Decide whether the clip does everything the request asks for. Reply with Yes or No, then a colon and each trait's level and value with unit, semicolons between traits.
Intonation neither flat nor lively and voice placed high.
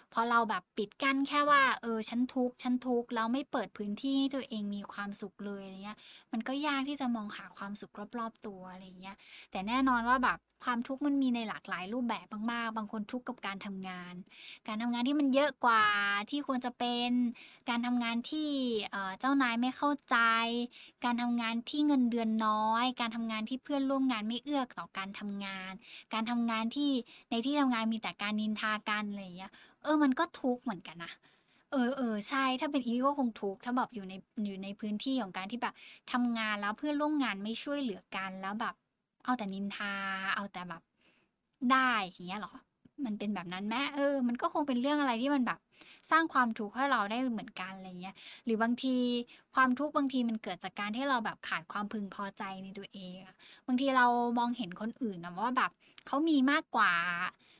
Yes: average, 4.1 semitones; high, 235 Hz